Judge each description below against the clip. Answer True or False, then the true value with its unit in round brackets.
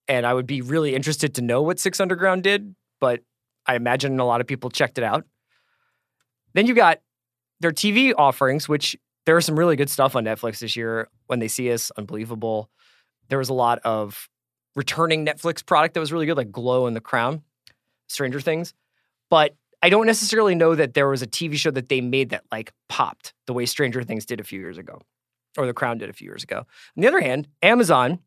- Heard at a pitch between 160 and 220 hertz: False (135 Hz)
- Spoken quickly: True (215 wpm)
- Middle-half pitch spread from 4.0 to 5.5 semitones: True (5.1 semitones)